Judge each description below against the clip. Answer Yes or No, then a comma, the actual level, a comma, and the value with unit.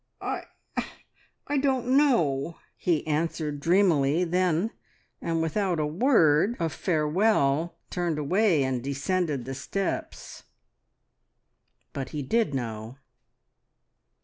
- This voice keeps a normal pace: No, slow, 95 wpm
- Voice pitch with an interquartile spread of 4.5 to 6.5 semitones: Yes, average, 4.9 semitones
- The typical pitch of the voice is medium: Yes, medium, 165 Hz